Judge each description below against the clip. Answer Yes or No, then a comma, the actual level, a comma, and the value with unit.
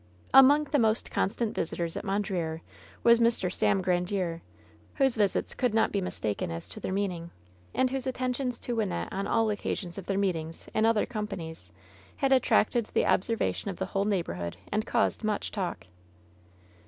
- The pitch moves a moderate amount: Yes, average, 4.7 semitones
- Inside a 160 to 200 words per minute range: Yes, average, 165 wpm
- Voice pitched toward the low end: No, high, 205 Hz